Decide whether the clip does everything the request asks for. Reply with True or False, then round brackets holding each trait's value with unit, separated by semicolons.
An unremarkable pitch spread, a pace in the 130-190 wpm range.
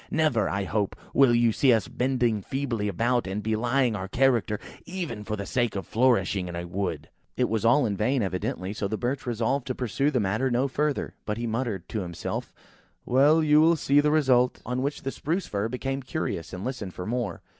False (4.5 semitones; 205 wpm)